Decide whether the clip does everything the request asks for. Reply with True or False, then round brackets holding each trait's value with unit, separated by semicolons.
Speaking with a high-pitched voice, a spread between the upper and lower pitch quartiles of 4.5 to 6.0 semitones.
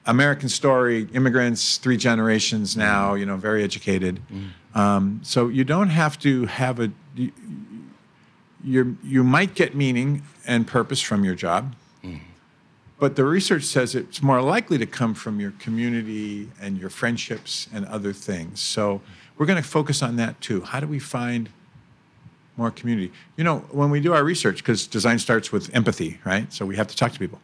False (120 Hz; 5.0 semitones)